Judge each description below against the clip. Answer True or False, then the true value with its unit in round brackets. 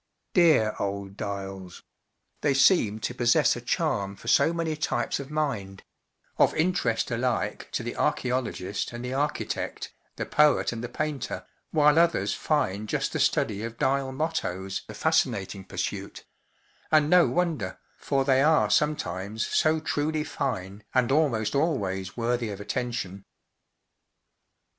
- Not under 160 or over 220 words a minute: False (140 wpm)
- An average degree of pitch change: False (7.0 semitones)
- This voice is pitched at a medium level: False (125 Hz)